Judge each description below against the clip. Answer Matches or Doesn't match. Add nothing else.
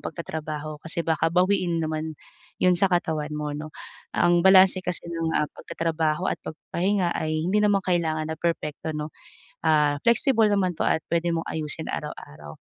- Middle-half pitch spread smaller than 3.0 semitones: Matches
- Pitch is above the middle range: Doesn't match